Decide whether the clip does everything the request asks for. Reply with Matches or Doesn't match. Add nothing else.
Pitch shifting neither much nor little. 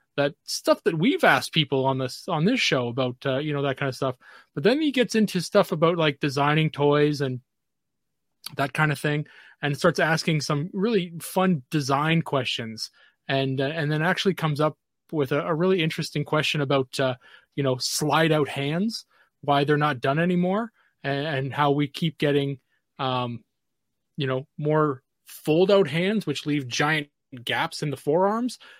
Matches